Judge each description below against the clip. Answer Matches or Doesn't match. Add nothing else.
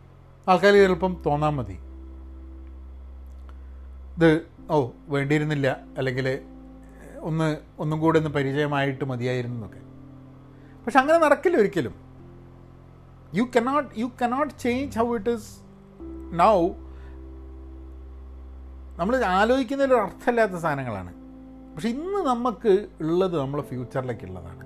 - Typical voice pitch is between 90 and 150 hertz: Matches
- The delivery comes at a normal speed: Matches